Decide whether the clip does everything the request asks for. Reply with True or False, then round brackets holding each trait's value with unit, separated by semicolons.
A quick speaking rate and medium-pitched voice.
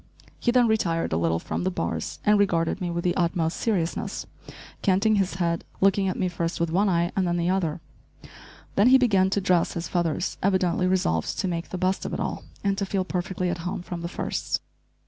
True (215 wpm; 180 Hz)